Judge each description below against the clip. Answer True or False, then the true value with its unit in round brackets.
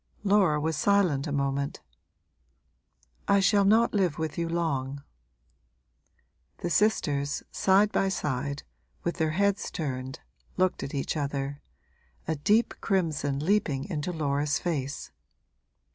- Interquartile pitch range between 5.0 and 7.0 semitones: True (5.3 semitones)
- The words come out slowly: True (120 wpm)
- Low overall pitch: False (155 Hz)